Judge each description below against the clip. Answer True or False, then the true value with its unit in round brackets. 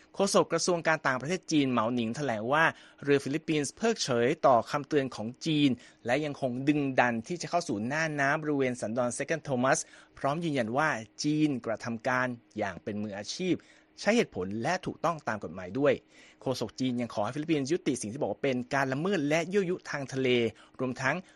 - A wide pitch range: False (3.9 semitones)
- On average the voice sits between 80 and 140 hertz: True (135 Hz)